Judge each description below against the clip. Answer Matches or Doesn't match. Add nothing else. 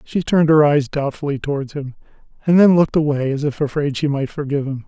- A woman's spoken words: Doesn't match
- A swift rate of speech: Matches